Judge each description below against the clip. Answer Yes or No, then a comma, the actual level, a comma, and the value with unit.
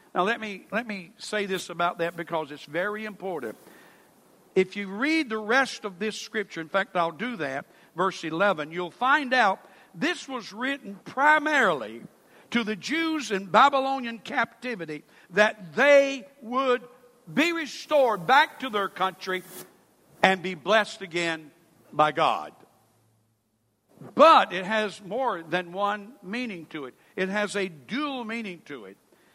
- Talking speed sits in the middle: Yes, average, 145 wpm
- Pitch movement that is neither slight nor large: No, wide, 5.9 semitones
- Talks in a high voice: Yes, high, 205 Hz